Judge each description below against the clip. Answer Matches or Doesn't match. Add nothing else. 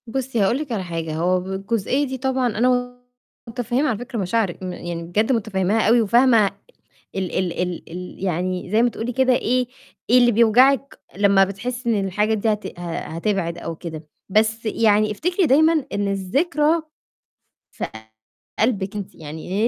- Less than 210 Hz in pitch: Doesn't match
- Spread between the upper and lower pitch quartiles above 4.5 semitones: Matches